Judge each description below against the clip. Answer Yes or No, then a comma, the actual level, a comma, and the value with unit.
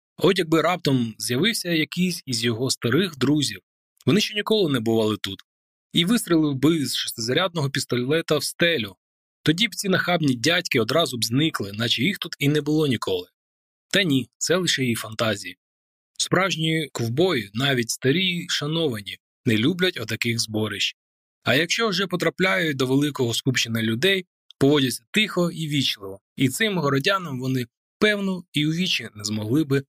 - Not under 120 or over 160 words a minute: Yes, fast, 155 wpm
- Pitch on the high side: No, medium, 140 Hz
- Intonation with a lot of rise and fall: Yes, wide, 7.0 semitones